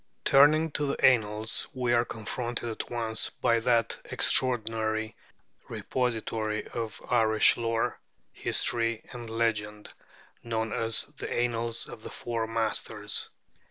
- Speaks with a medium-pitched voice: No, low, 115 Hz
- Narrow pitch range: Yes, narrow, 1.4 semitones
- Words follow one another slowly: Yes, slow, 120 wpm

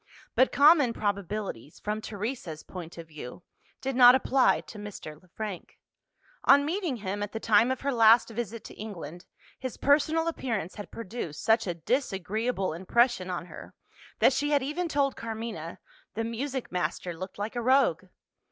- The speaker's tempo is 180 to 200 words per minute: No, average, 165 wpm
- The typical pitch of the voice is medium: No, high, 225 Hz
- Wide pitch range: Yes, wide, 5.7 semitones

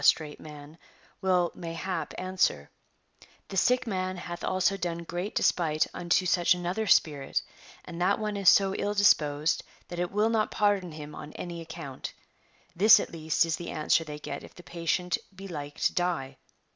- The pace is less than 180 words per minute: No, average, 185 wpm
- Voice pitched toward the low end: No, medium, 175 Hz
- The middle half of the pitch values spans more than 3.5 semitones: No, average, 3.2 semitones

